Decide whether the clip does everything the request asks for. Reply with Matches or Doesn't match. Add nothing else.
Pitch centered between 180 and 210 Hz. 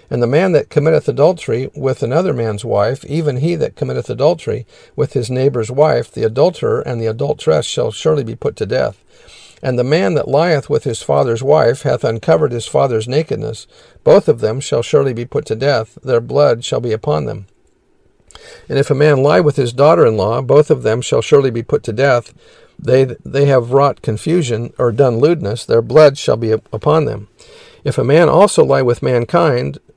Doesn't match